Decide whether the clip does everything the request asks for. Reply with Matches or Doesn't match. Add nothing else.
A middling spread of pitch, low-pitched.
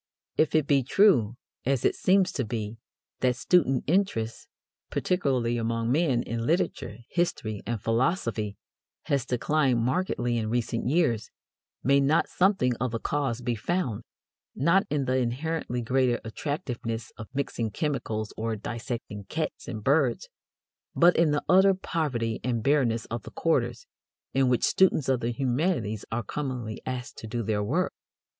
Matches